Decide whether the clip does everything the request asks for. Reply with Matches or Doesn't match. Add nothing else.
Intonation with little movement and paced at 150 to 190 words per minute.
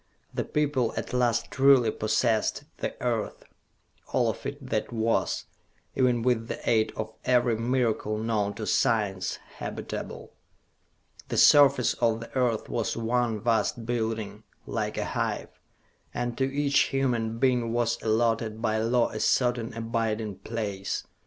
Doesn't match